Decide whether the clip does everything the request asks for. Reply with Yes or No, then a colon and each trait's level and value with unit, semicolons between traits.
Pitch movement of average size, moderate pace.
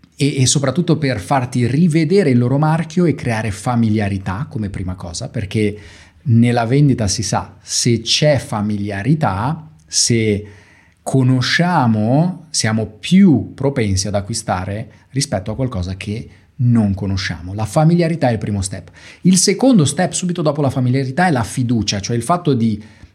No: wide, 6.0 semitones; average, 145 wpm